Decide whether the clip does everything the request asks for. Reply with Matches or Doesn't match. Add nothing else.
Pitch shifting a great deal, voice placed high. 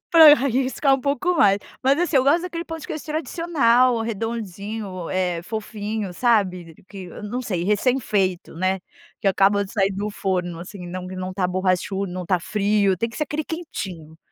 Matches